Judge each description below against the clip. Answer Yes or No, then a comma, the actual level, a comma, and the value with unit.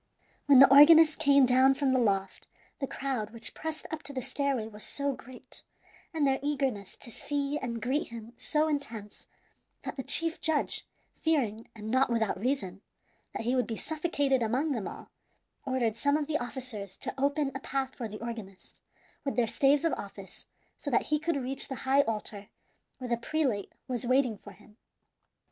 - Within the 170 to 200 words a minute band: Yes, average, 185 wpm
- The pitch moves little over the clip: No, average, 3.8 semitones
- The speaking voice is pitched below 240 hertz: No, very high, 260 Hz